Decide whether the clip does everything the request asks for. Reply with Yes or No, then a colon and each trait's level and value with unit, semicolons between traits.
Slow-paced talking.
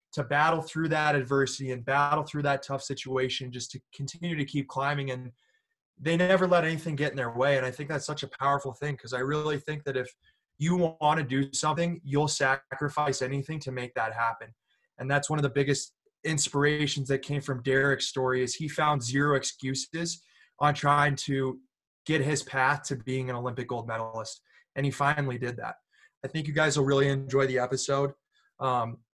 No: average, 200 wpm